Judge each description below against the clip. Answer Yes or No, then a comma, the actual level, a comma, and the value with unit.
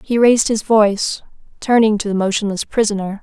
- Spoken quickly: No, average, 165 wpm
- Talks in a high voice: Yes, high, 215 Hz